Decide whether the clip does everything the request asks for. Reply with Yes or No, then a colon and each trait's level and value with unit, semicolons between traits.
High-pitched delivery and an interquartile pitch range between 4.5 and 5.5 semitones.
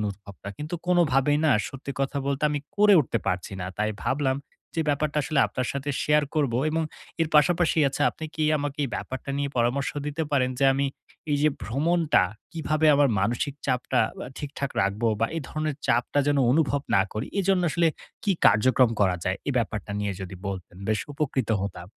No: medium, 140 Hz; average, 4.8 semitones